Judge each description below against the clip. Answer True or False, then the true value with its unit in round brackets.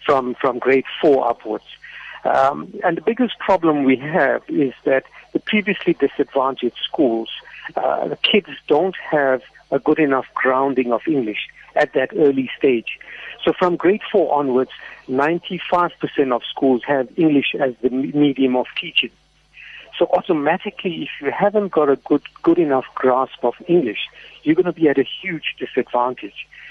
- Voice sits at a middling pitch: True (145 Hz)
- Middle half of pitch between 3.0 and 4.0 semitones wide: False (5.2 semitones)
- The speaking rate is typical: True (155 wpm)